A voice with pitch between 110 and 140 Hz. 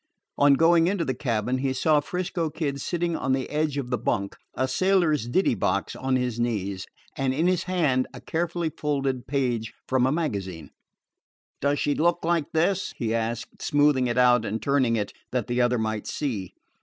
Yes: low, 135 Hz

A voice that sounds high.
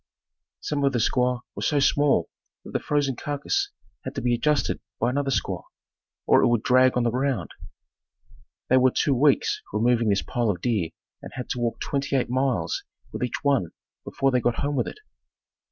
No: low, 125 Hz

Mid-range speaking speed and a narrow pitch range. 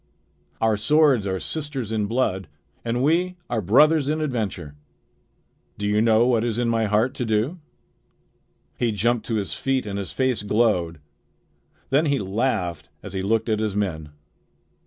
No: average, 160 wpm; average, 4.2 semitones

